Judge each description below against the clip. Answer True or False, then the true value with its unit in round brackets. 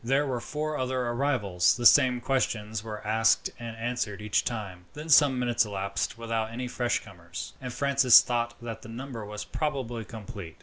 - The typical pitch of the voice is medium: False (120 Hz)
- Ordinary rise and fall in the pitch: True (3.1 semitones)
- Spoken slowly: False (175 wpm)